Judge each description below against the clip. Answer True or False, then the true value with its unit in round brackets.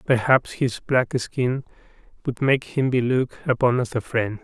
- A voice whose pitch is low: True (125 Hz)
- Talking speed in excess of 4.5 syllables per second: False (4.4 syllables/s)